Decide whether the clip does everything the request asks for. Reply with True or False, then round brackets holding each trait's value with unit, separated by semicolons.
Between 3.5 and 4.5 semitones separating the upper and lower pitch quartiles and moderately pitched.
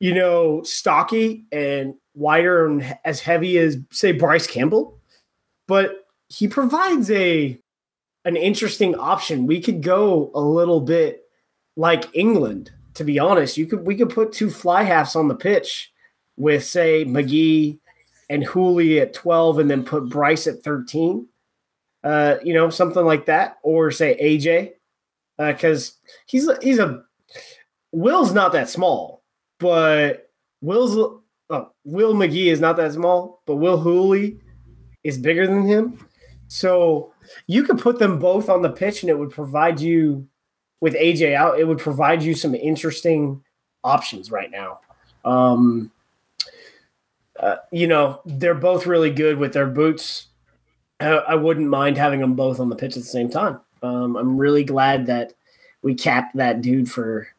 True (3.9 semitones; 160 Hz)